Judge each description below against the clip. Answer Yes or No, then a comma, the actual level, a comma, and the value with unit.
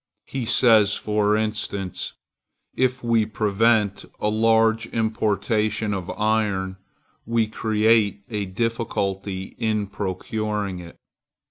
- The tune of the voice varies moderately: No, narrow, 1.8 semitones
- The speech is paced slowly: Yes, slow, 100 wpm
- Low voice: Yes, low, 105 Hz